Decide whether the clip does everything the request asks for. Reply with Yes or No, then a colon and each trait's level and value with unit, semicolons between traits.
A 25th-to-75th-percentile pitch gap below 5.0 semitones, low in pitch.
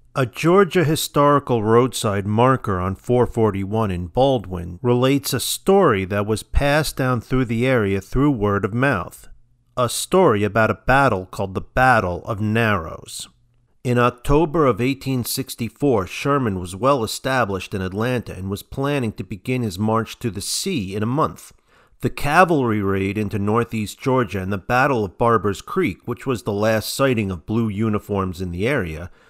Yes: average, 4.4 semitones; low, 115 Hz